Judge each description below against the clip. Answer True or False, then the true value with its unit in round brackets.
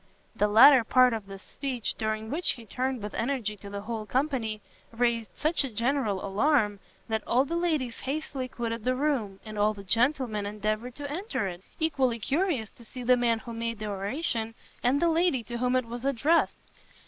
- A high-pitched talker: True (235 Hz)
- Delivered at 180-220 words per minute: True (195 wpm)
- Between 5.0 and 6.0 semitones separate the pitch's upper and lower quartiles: False (4.0 semitones)